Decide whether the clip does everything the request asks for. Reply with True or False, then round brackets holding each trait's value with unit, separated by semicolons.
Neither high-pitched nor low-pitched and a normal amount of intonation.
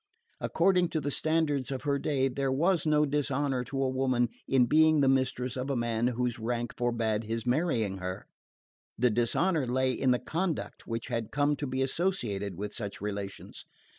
False (130 Hz; 3.8 semitones)